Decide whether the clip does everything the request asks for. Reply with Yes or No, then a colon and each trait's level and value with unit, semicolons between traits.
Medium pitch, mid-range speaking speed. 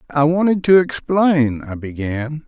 Yes: medium, 150 Hz; average, 145 wpm